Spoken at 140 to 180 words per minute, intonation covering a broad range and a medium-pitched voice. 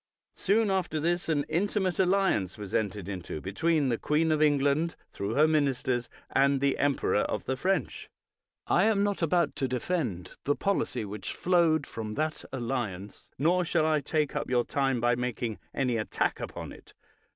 Yes: average, 170 wpm; wide, 5.7 semitones; medium, 145 Hz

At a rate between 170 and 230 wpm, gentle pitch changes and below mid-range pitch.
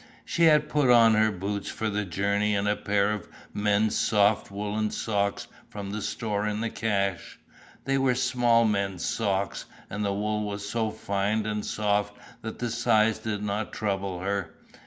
Yes: average, 175 wpm; narrow, 1.5 semitones; low, 105 Hz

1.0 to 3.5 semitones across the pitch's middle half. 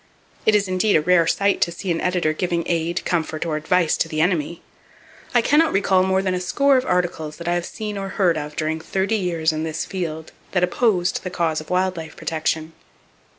Yes: average, 2.9 semitones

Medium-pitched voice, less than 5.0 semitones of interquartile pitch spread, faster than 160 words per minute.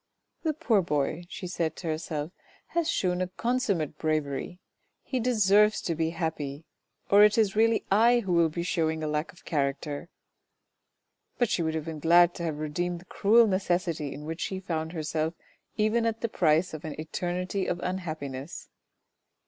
Yes: medium, 175 Hz; average, 4.2 semitones; average, 180 wpm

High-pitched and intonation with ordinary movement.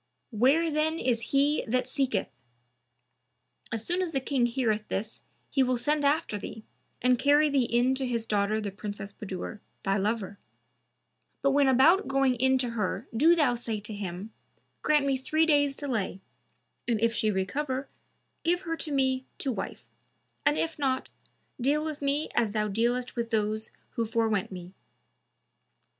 Yes: very high, 250 Hz; average, 4.7 semitones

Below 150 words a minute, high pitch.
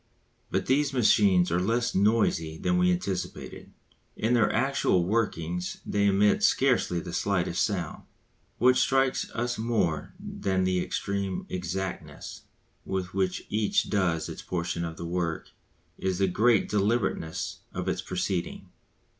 No: slow, 135 wpm; very low, 95 Hz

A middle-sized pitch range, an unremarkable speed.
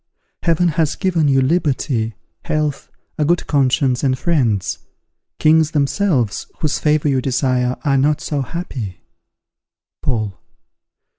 No: average, 3.4 semitones; slow, 120 wpm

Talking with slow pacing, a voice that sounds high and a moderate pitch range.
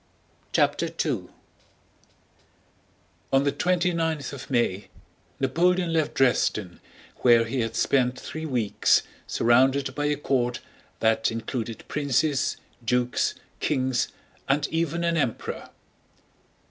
No: slow, 110 wpm; low, 135 Hz; average, 4.3 semitones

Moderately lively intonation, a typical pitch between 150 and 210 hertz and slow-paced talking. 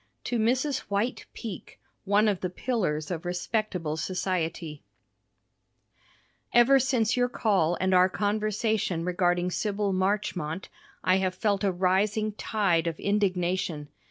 Yes: average, 3.3 semitones; high, 190 Hz; slow, 125 wpm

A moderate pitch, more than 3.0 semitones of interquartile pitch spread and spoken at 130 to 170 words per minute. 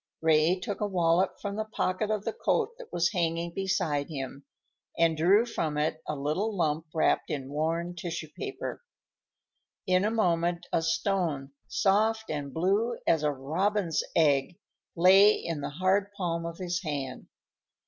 Yes: medium, 170 Hz; average, 3.9 semitones; average, 160 wpm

